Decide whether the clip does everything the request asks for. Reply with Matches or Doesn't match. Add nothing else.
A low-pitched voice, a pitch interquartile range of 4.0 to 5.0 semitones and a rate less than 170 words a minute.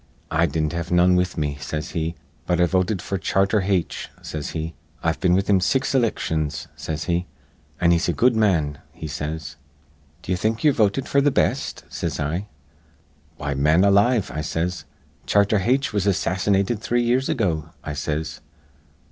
Doesn't match